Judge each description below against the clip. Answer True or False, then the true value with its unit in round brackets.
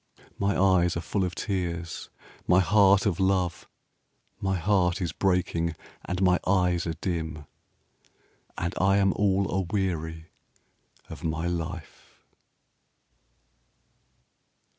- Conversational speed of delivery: False (115 wpm)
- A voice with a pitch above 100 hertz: False (90 Hz)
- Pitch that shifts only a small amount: True (2.3 semitones)